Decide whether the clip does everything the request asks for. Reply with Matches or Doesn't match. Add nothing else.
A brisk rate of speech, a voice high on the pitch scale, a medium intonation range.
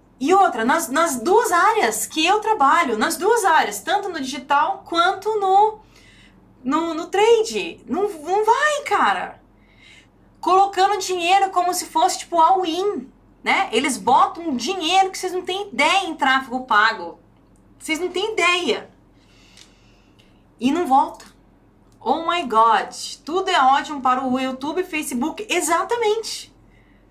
Doesn't match